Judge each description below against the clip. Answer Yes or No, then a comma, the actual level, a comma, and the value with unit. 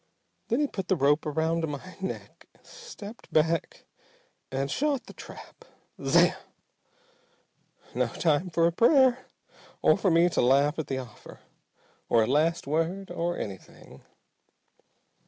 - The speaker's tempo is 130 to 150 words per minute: Yes, slow, 135 wpm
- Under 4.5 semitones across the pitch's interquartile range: No, average, 4.9 semitones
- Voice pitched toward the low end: No, medium, 165 Hz